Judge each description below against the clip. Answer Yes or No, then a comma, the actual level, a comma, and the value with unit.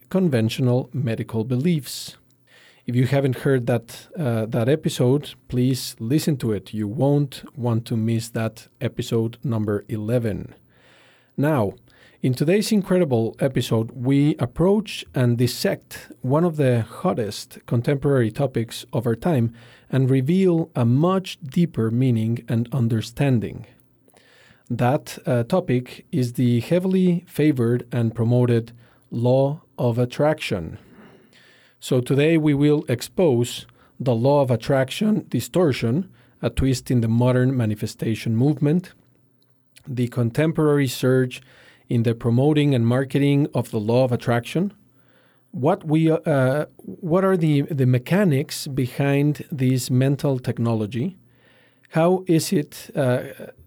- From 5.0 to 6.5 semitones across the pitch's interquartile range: No, average, 3.7 semitones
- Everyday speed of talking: No, slow, 120 wpm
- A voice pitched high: No, low, 130 Hz